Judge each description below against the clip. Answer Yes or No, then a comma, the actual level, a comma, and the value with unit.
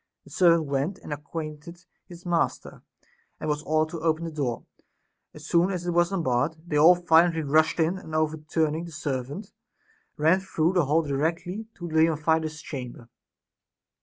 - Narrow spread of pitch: Yes, narrow, 2.2 semitones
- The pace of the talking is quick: No, average, 165 wpm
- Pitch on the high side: No, medium, 160 Hz